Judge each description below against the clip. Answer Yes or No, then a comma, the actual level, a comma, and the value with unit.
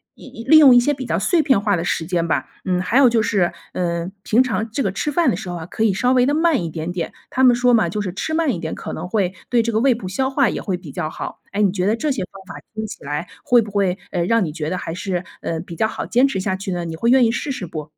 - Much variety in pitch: Yes, wide, 5.7 semitones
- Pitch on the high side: Yes, high, 205 Hz